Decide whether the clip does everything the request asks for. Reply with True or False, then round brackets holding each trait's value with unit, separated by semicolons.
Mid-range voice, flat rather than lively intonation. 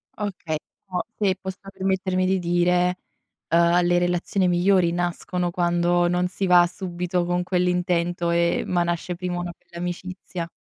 True (175 Hz; 0.9 semitones)